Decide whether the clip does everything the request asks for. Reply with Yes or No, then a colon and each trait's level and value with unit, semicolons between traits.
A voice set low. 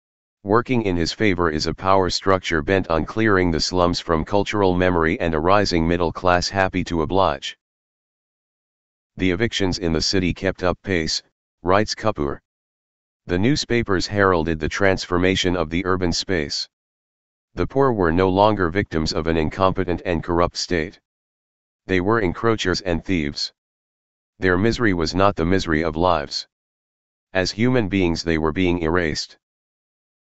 Yes: very low, 90 Hz